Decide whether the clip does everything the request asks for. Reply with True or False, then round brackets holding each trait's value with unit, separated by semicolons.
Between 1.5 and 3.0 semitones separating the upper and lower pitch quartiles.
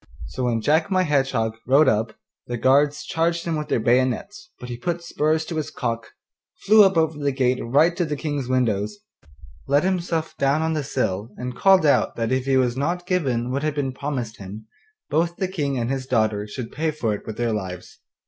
False (5.0 semitones)